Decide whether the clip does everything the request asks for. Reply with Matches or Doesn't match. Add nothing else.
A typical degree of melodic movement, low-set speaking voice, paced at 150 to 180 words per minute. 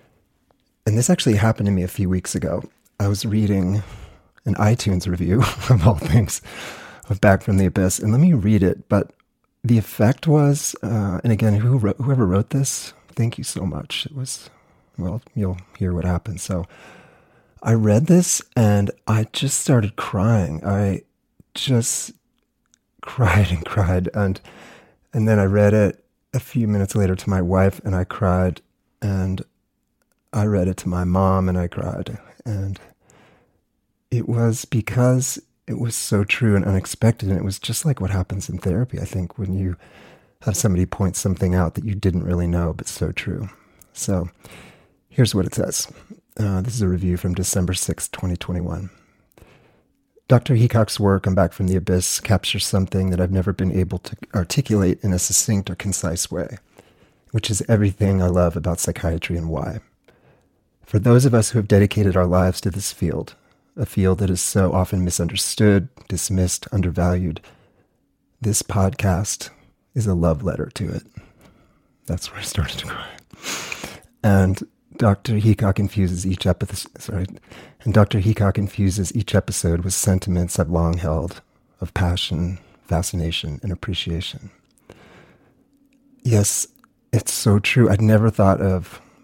Matches